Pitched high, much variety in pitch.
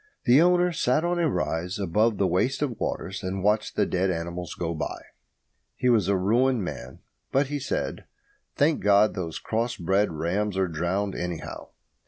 No: low, 100 Hz; wide, 5.8 semitones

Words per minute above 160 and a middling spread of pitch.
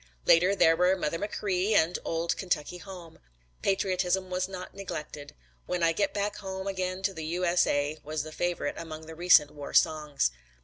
Yes: average, 170 wpm; average, 3.0 semitones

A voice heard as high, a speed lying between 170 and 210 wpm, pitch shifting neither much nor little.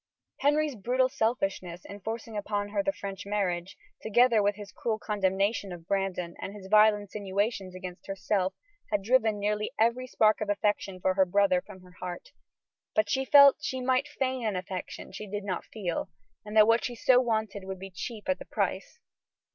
Yes: high, 205 Hz; average, 185 wpm; average, 3.1 semitones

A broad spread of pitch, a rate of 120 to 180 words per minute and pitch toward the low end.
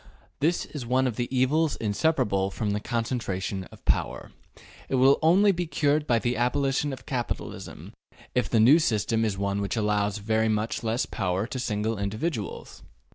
No: average, 4.4 semitones; average, 170 wpm; low, 115 Hz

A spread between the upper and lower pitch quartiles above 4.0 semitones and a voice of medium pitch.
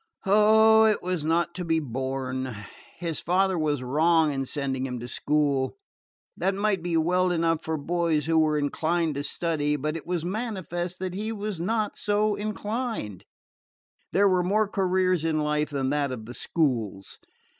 Yes: average, 4.4 semitones; medium, 165 Hz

